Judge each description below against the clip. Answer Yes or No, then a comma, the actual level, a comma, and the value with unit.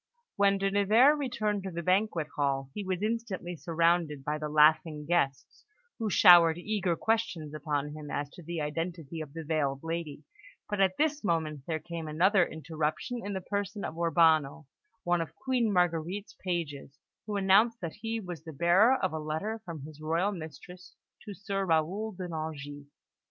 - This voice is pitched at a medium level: Yes, medium, 170 Hz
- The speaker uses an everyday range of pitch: Yes, average, 4.3 semitones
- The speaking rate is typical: Yes, average, 170 wpm